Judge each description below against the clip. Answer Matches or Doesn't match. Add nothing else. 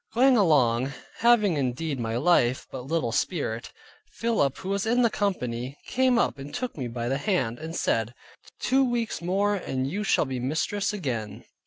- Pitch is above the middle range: Doesn't match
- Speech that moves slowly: Doesn't match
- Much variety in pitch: Matches